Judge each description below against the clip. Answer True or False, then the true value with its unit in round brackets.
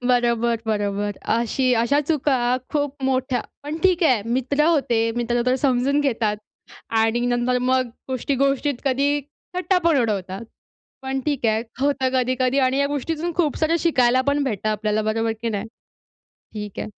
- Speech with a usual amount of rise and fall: True (3.6 semitones)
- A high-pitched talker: True (255 Hz)